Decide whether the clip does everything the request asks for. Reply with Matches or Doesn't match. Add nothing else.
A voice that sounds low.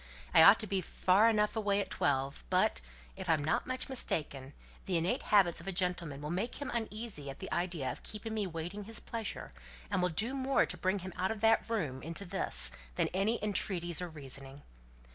Doesn't match